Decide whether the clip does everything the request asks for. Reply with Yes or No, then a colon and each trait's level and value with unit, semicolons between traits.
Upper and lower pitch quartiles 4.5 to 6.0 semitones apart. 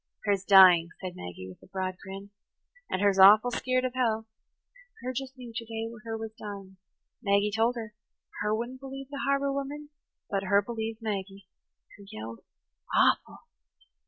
No: average, 4.0 semitones